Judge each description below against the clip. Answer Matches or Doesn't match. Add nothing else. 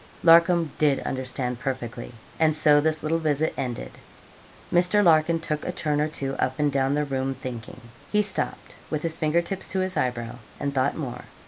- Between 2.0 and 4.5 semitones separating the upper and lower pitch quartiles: Matches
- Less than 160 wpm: Doesn't match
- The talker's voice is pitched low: Doesn't match